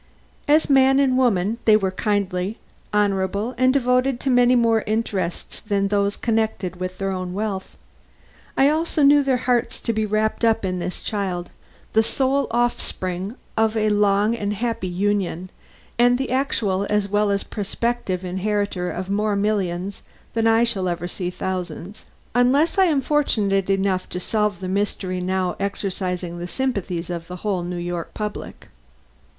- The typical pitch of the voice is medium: No, high, 205 Hz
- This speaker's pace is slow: No, average, 160 wpm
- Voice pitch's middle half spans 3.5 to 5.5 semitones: Yes, average, 4.0 semitones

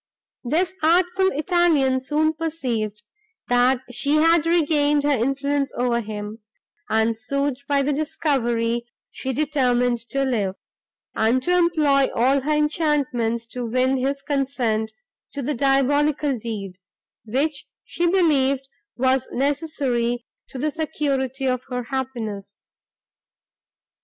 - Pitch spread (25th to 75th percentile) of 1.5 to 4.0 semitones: Yes, average, 3.7 semitones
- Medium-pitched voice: No, very high, 270 Hz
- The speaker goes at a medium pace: No, slow, 115 wpm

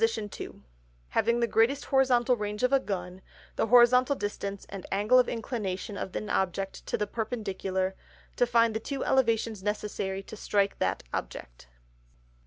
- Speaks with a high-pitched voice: Yes, high, 215 Hz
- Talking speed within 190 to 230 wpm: No, average, 155 wpm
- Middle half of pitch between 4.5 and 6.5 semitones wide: No, average, 3.5 semitones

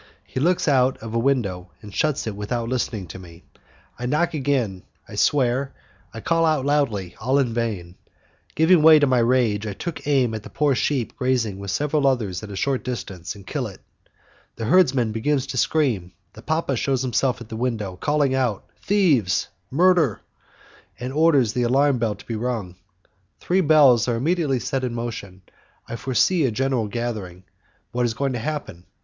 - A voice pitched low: Yes, low, 125 Hz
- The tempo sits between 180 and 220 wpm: Yes, average, 185 wpm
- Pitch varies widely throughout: No, average, 4.5 semitones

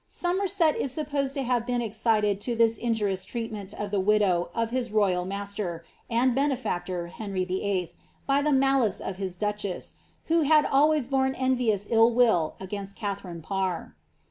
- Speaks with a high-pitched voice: Yes, high, 220 Hz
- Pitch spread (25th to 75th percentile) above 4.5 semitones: Yes, average, 5.2 semitones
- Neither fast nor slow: Yes, average, 165 wpm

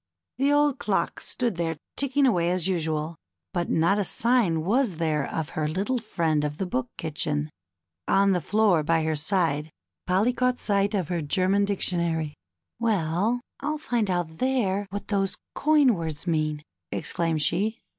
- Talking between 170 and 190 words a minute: No, average, 160 wpm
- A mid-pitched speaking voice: Yes, medium, 180 Hz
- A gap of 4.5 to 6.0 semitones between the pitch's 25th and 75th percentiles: Yes, average, 5.2 semitones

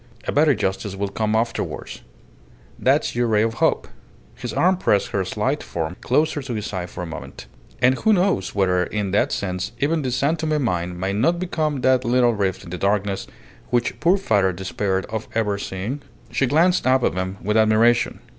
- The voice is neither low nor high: No, low, 110 Hz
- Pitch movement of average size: No, wide, 6.0 semitones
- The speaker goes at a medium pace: Yes, average, 195 wpm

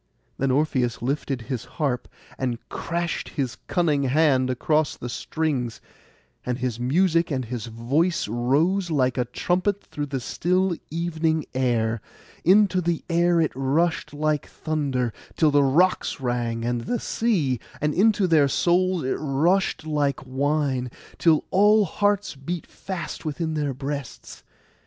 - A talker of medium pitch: Yes, medium, 150 Hz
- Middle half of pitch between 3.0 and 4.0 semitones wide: No, average, 5.0 semitones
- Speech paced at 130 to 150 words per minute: Yes, average, 140 wpm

